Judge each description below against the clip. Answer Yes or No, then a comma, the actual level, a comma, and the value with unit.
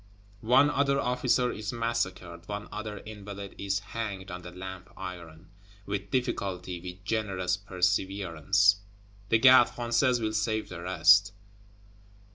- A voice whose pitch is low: Yes, low, 100 Hz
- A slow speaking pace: Yes, slow, 125 wpm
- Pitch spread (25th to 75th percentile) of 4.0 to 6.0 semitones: No, average, 3.6 semitones